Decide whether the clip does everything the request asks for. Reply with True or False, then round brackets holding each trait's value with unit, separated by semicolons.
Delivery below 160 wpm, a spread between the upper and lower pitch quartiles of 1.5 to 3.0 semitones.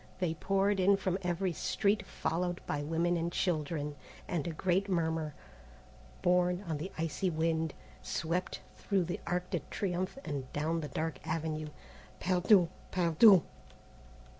True (140 wpm; 2.5 semitones)